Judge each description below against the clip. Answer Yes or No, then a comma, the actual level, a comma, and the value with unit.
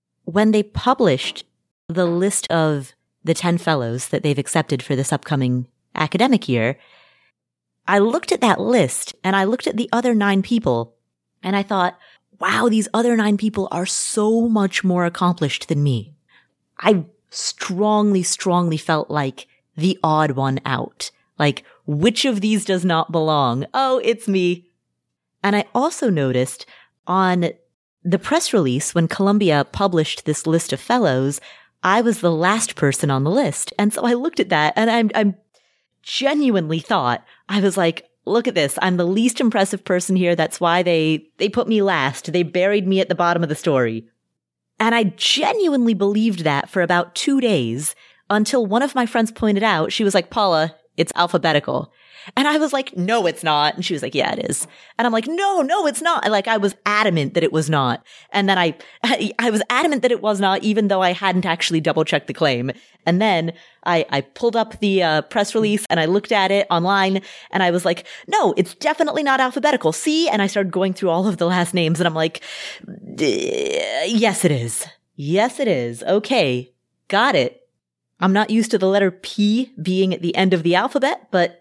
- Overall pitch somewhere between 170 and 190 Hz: Yes, medium, 185 Hz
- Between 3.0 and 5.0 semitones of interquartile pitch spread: No, wide, 5.4 semitones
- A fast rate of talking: No, average, 190 wpm